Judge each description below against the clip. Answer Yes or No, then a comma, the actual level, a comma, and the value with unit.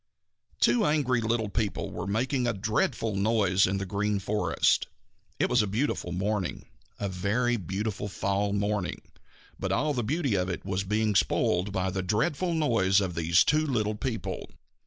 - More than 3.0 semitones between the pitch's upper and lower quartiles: Yes, average, 3.5 semitones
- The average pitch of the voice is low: Yes, low, 105 Hz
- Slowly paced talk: No, average, 165 wpm